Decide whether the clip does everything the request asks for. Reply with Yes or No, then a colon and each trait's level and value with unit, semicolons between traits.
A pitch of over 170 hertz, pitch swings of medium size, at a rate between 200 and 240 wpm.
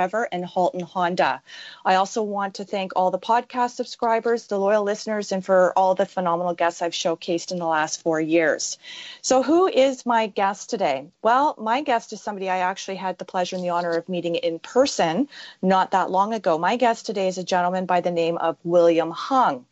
Yes: high, 190 Hz; average, 4.3 semitones; fast, 205 wpm